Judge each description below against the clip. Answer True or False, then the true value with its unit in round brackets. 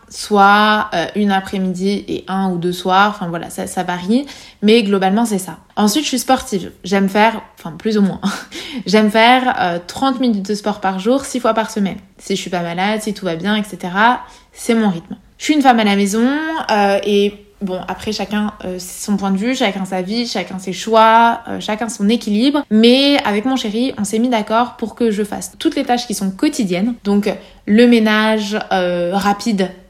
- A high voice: True (210 Hz)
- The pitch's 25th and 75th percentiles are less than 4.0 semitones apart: True (3.2 semitones)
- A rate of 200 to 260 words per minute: True (210 wpm)